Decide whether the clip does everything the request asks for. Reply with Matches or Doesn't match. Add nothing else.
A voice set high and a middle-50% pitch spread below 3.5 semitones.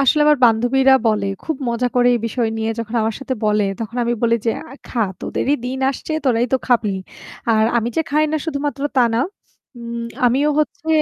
Matches